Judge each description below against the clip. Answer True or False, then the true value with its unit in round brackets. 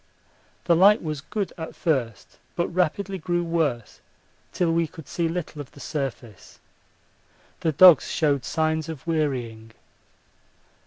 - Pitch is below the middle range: False (160 Hz)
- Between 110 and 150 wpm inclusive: True (135 wpm)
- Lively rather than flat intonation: False (3.6 semitones)